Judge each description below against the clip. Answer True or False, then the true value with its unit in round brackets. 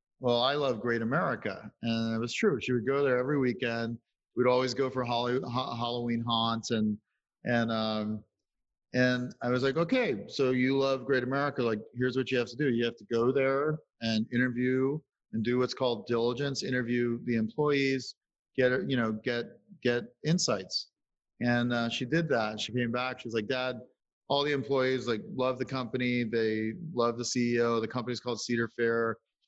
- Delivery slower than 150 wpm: False (185 wpm)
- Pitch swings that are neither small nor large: False (1.9 semitones)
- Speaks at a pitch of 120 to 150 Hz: True (125 Hz)